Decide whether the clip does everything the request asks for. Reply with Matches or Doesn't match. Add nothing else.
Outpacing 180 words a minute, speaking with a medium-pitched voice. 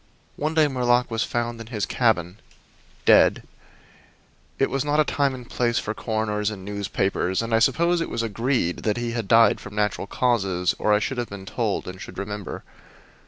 Doesn't match